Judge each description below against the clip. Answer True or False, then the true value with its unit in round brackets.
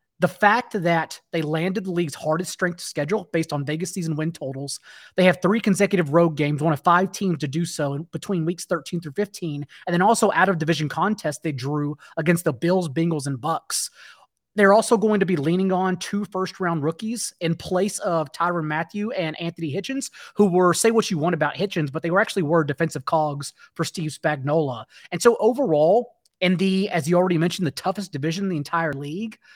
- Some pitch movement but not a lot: True (3.5 semitones)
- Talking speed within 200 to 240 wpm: True (205 wpm)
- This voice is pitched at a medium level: True (175 Hz)